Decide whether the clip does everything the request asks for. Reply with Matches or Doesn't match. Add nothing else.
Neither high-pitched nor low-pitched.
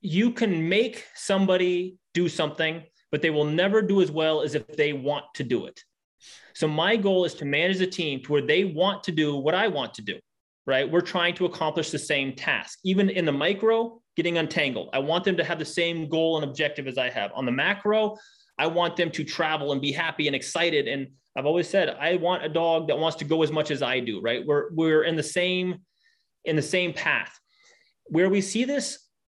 Matches